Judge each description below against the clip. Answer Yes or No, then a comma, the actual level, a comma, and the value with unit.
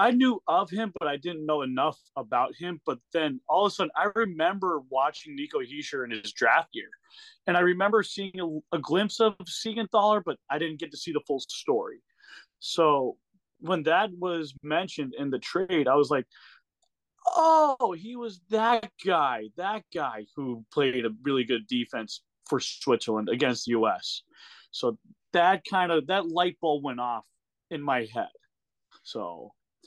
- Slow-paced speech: No, average, 175 wpm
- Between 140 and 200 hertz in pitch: Yes, medium, 185 Hz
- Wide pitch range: Yes, wide, 7.5 semitones